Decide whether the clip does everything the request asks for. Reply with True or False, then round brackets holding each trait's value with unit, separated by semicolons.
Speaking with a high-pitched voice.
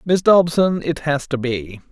False (150 Hz)